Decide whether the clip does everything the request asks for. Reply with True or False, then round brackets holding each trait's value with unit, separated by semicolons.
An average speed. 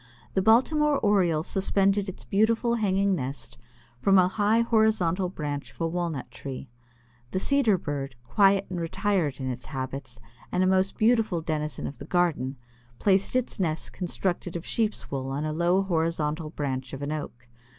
True (165 wpm)